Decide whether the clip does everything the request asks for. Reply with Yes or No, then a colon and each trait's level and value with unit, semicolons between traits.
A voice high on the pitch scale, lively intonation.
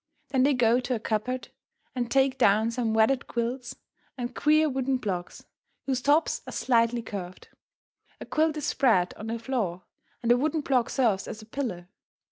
No: high, 245 Hz; average, 3.2 semitones